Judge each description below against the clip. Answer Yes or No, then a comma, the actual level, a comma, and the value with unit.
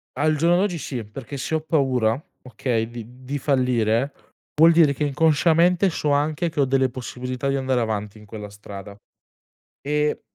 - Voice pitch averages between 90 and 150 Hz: Yes, low, 135 Hz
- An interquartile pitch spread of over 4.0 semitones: Yes, average, 4.5 semitones